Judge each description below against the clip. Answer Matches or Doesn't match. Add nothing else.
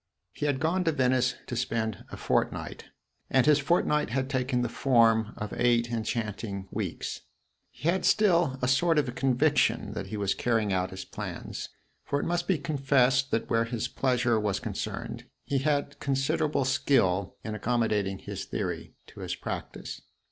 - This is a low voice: Matches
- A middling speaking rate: Matches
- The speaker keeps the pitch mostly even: Doesn't match